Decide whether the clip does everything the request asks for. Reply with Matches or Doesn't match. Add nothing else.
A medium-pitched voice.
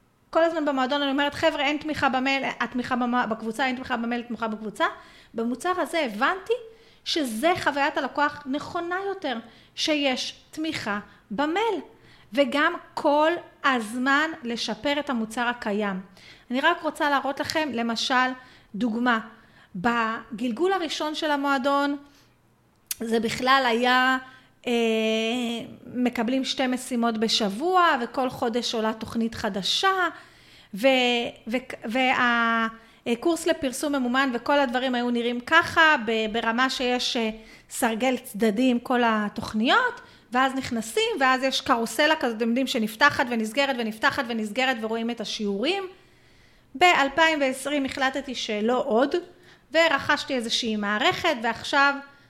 Doesn't match